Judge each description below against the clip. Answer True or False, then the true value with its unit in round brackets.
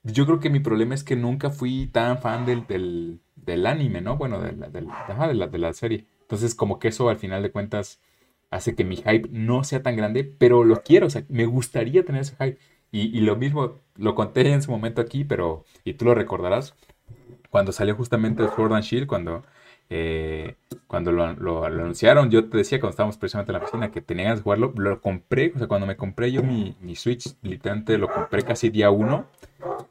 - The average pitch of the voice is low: True (115 Hz)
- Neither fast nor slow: False (225 wpm)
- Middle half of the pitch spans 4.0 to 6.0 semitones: False (3.5 semitones)